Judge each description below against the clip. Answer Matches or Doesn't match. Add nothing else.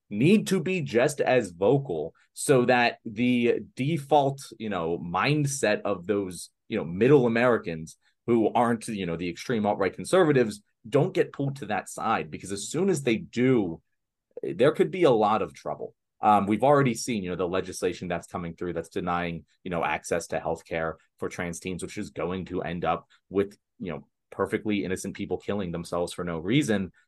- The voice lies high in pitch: Doesn't match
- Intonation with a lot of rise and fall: Matches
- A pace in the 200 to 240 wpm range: Doesn't match